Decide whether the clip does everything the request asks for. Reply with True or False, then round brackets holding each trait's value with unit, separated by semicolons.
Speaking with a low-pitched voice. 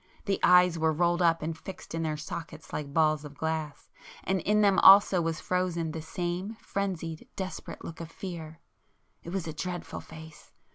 False (165 Hz)